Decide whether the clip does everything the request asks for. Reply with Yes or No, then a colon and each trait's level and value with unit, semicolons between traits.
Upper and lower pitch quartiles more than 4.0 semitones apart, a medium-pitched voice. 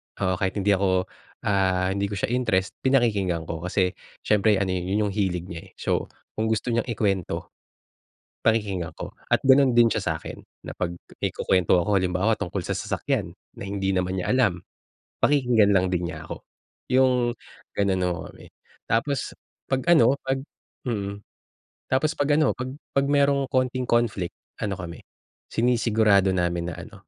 No: average, 4.8 semitones; low, 100 Hz